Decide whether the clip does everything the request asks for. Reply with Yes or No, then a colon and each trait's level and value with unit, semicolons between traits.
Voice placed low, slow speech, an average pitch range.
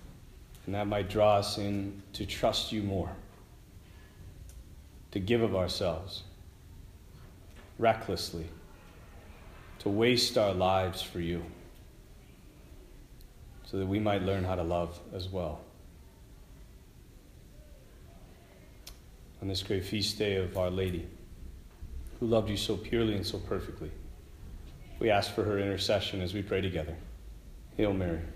Yes: very low, 95 Hz; slow, 125 wpm; average, 3.1 semitones